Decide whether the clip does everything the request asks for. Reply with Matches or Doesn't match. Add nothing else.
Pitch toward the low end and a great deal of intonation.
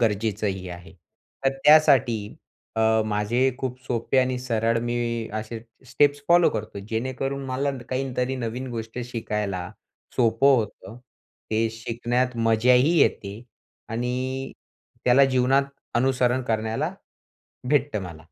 Doesn't match